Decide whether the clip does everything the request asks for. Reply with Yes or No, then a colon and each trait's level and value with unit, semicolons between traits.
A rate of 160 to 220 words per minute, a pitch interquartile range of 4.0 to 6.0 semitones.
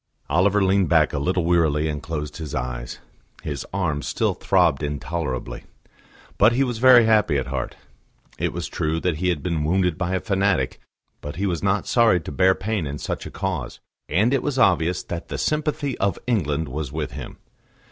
Yes: average, 190 wpm; average, 5.1 semitones